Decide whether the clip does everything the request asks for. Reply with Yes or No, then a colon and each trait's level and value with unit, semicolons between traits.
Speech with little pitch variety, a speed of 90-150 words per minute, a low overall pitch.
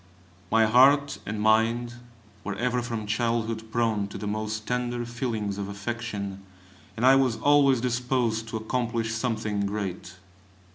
Yes: narrow, 2.3 semitones; average, 140 wpm; low, 115 Hz